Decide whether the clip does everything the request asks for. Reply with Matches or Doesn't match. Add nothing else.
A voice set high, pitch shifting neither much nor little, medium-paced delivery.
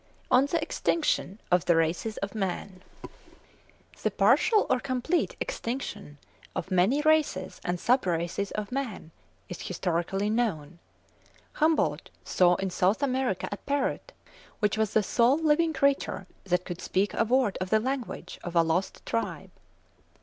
Doesn't match